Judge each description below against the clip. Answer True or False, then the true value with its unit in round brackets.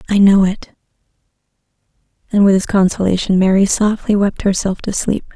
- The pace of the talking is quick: False (145 wpm)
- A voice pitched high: True (195 Hz)